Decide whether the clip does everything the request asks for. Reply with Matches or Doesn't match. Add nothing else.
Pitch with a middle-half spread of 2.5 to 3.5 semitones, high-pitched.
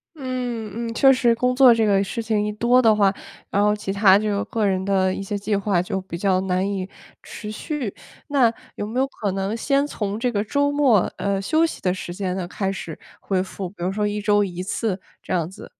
Matches